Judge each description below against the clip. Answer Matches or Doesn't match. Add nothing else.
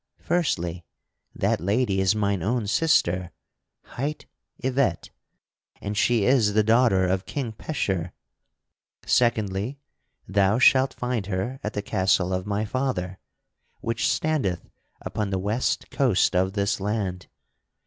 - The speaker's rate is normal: Doesn't match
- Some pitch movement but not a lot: Matches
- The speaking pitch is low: Matches